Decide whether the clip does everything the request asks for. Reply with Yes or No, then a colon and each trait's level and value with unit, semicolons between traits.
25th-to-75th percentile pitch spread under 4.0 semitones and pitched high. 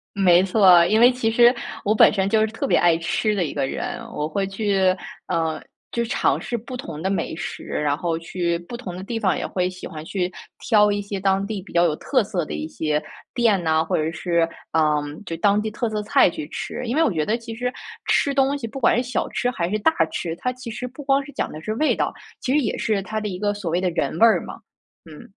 No: average, 5.1 semitones; high, 200 Hz